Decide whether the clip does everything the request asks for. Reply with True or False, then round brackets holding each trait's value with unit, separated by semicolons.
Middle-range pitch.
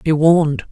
True (160 Hz)